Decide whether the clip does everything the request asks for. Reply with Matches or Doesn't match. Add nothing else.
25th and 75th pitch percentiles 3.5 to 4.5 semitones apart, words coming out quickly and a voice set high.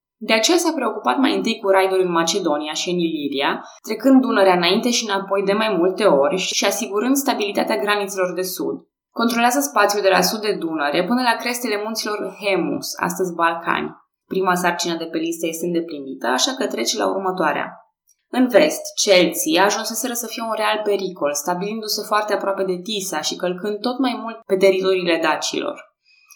Matches